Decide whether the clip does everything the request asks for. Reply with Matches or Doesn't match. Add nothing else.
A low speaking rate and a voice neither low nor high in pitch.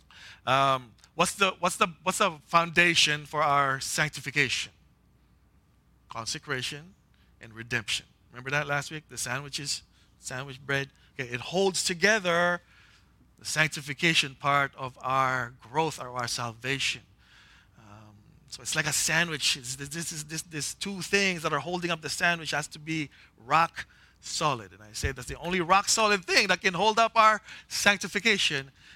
Doesn't match